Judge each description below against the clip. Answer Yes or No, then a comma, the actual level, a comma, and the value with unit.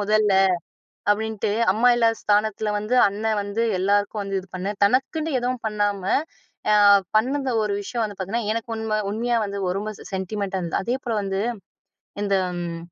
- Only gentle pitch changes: Yes, narrow, 2.1 semitones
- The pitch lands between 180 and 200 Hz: No, high, 210 Hz